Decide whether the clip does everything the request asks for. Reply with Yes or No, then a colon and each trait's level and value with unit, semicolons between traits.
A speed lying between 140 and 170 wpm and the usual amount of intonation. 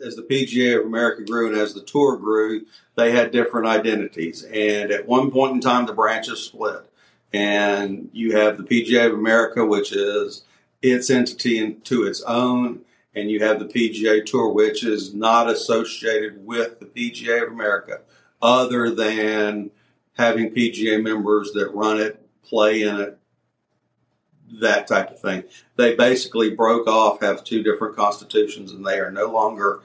No: average, 165 wpm; narrow, 2.2 semitones